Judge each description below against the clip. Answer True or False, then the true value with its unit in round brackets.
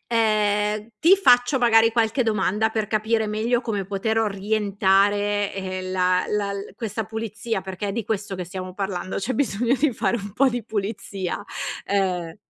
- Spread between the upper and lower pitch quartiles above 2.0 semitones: True (2.5 semitones)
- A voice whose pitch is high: True (210 Hz)